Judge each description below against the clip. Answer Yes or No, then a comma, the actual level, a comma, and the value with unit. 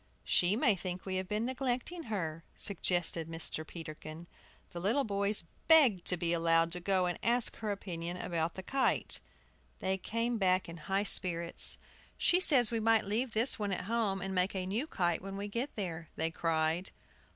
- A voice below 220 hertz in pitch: Yes, high, 190 Hz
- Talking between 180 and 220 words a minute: Yes, average, 185 wpm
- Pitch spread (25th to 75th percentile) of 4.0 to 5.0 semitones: Yes, average, 4.6 semitones